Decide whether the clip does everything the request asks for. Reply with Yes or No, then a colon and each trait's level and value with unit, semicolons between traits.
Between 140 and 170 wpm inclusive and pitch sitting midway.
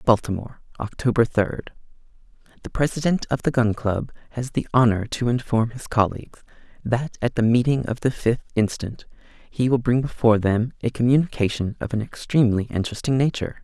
No: average, 160 wpm; low, 120 Hz